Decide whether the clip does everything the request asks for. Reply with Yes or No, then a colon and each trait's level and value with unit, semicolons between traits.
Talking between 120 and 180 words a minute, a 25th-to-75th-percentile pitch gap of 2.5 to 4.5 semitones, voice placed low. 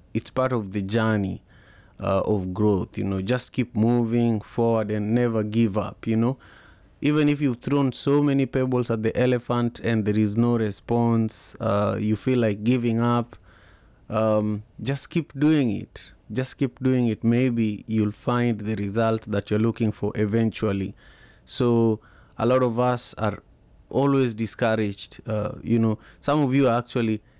Yes: average, 165 wpm; average, 2.8 semitones; low, 115 Hz